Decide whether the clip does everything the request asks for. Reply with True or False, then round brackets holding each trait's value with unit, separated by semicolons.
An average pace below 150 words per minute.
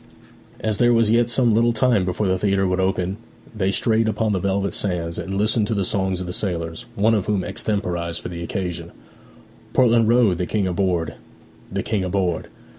False (190 wpm)